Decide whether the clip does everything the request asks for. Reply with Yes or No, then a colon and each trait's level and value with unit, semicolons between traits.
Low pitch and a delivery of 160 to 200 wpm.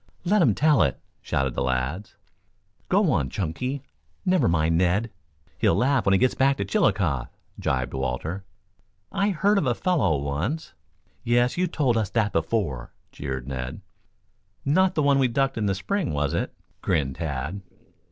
Yes: low, 100 Hz; average, 165 wpm